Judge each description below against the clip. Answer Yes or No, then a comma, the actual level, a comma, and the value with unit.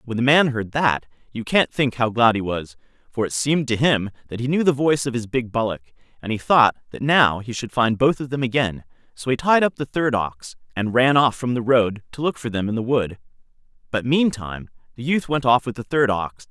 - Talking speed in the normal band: No, fast, 245 wpm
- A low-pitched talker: Yes, low, 125 Hz